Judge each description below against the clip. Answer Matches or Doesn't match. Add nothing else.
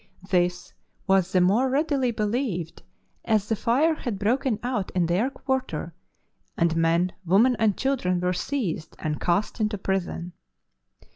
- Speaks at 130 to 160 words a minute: Matches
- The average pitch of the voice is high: Matches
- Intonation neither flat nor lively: Doesn't match